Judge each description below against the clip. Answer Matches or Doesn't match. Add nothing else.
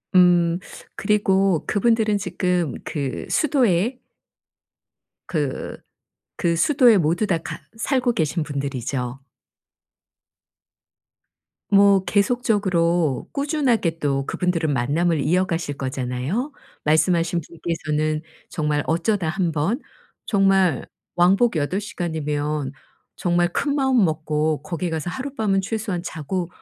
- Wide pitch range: Doesn't match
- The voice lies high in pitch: Doesn't match